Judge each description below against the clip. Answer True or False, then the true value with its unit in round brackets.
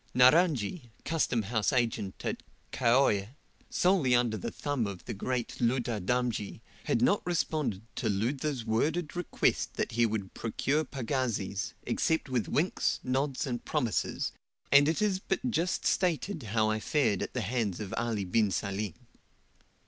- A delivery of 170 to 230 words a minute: False (150 wpm)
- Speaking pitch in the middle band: False (120 Hz)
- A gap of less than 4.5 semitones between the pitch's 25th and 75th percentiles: False (5.2 semitones)